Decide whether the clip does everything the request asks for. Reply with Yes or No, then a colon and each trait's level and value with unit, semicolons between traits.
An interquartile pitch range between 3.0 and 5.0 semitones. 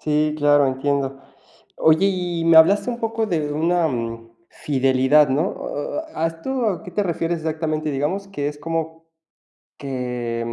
Yes: average, 3.3 semitones